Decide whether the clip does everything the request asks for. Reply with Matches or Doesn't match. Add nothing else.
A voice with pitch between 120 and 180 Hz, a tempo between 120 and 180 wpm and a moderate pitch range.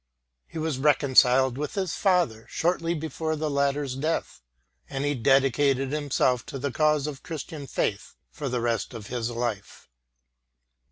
Matches